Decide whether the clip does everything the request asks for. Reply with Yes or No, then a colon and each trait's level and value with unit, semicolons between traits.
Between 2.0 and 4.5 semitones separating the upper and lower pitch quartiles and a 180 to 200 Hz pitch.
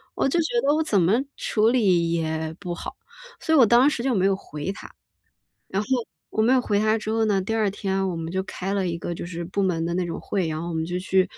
Yes: average, 4.2 semitones; high, 190 Hz